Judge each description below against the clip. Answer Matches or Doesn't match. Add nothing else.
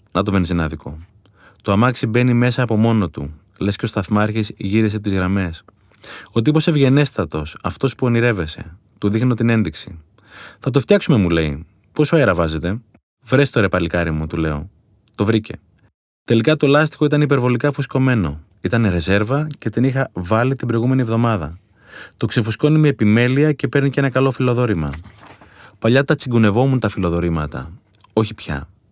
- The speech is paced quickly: Doesn't match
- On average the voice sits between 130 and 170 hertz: Doesn't match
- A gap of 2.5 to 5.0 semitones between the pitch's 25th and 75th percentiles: Doesn't match